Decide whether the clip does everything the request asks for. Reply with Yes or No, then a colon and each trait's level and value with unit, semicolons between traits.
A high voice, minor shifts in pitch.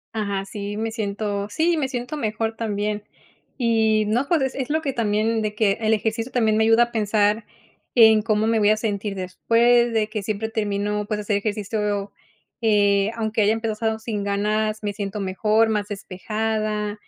Yes: high, 215 Hz; narrow, 1.5 semitones